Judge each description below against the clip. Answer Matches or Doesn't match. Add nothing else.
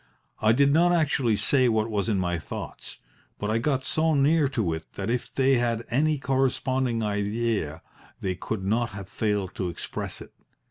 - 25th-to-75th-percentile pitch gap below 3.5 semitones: Doesn't match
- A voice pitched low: Matches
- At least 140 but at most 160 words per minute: Doesn't match